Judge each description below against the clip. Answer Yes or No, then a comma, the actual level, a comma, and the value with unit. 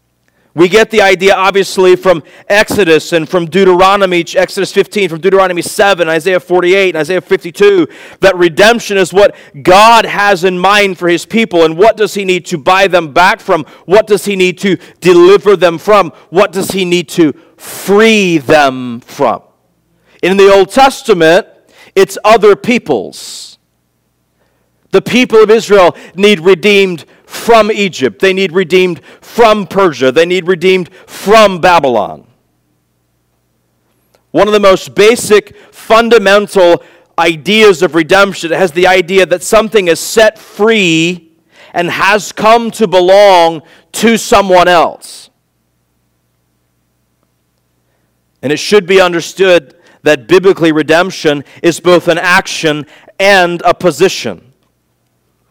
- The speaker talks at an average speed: No, slow, 130 wpm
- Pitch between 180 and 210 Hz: Yes, medium, 185 Hz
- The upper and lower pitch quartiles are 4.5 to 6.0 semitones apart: No, average, 3.8 semitones